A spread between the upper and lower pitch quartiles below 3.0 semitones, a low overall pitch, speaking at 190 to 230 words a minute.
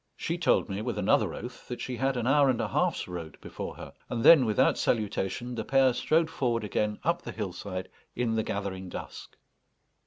No: average, 4.6 semitones; low, 120 Hz; average, 195 wpm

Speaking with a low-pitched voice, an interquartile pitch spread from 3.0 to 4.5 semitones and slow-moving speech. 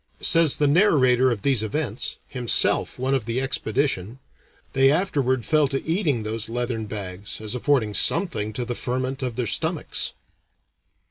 No: low, 125 Hz; average, 3.8 semitones; average, 150 wpm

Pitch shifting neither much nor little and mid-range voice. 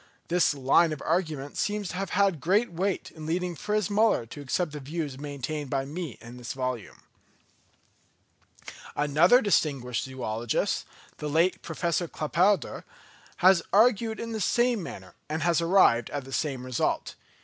No: wide, 5.7 semitones; medium, 160 Hz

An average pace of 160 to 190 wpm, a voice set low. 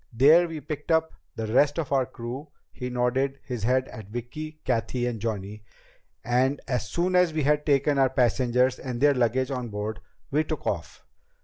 Yes: average, 185 wpm; low, 130 Hz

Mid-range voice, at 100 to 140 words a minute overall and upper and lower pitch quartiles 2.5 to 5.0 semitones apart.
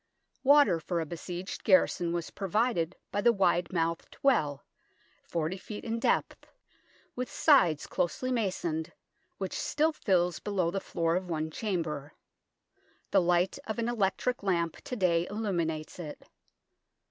Yes: medium, 180 Hz; slow, 135 wpm; average, 4.2 semitones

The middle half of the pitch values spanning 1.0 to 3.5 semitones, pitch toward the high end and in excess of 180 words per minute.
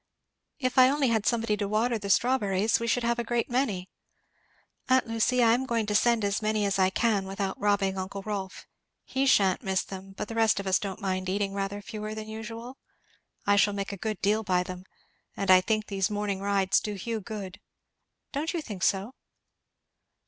Yes: average, 2.8 semitones; high, 210 Hz; average, 200 wpm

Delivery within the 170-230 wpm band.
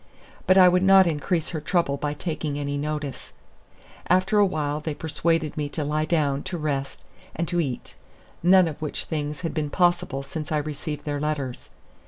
Yes: average, 180 wpm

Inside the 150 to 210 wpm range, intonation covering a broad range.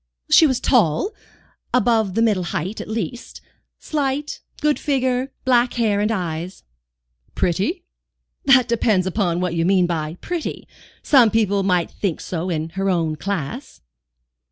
No: average, 140 wpm; wide, 6.0 semitones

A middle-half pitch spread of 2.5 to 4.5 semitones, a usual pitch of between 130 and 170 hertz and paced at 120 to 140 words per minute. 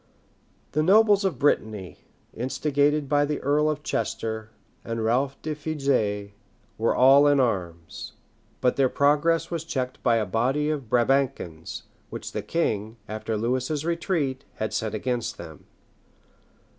No: average, 5.0 semitones; low, 135 Hz; slow, 135 wpm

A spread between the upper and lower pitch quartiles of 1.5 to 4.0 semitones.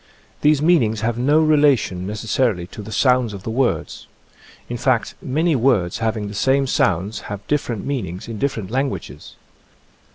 No: average, 4.7 semitones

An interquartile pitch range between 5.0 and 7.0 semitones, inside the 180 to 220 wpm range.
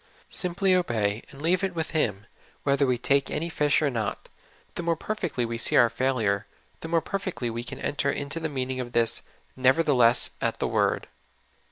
Yes: wide, 5.6 semitones; average, 190 wpm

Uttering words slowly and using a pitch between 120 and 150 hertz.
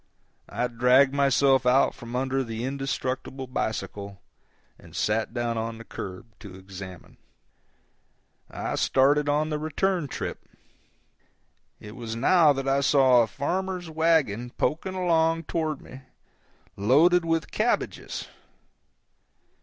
Yes: slow, 120 wpm; low, 135 Hz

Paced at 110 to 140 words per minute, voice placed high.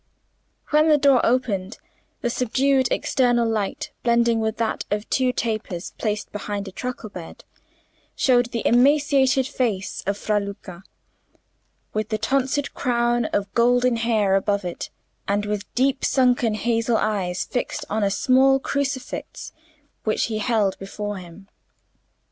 Yes: slow, 135 wpm; high, 230 Hz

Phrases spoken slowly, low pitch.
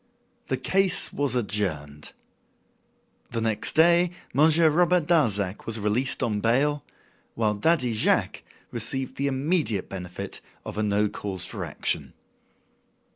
Yes: slow, 125 wpm; low, 120 Hz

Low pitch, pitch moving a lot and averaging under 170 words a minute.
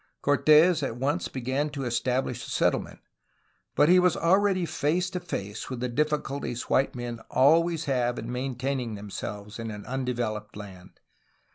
No: low, 130 Hz; average, 4.4 semitones; average, 155 wpm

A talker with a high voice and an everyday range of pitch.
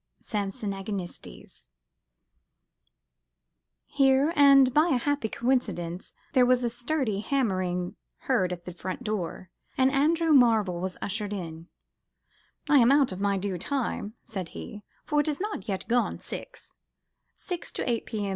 No: high, 225 Hz; wide, 6.3 semitones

